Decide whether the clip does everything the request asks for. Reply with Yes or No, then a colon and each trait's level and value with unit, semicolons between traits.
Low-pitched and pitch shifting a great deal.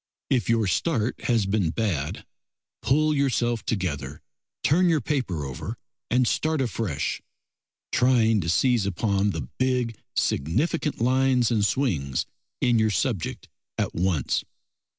Yes: low, 115 Hz; wide, 5.9 semitones